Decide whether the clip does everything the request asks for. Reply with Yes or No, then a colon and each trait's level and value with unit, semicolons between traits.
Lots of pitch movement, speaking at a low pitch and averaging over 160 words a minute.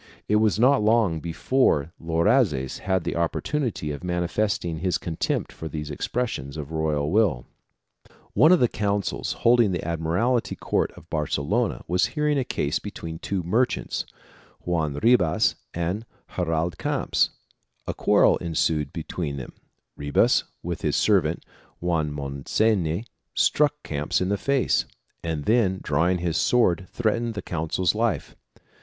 No: wide, 5.7 semitones; very low, 90 Hz; average, 140 wpm